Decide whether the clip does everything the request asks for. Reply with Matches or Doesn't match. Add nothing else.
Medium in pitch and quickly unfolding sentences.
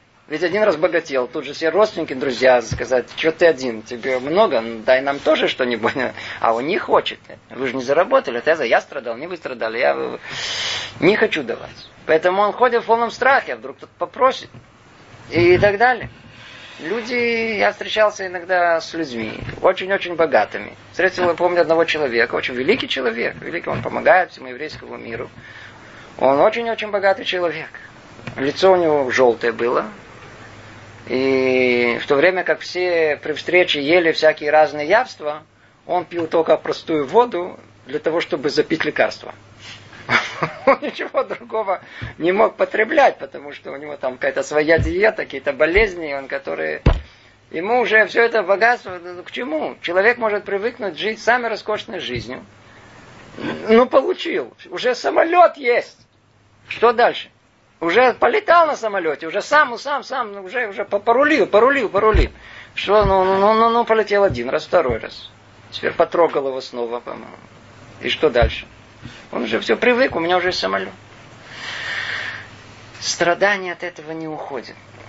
Doesn't match